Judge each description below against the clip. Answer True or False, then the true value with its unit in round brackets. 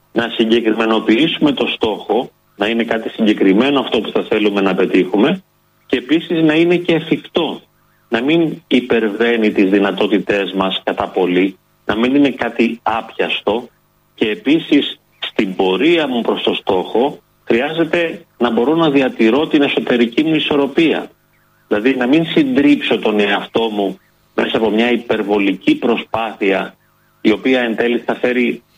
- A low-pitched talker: True (115 Hz)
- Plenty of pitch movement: True (6.1 semitones)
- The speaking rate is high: False (140 wpm)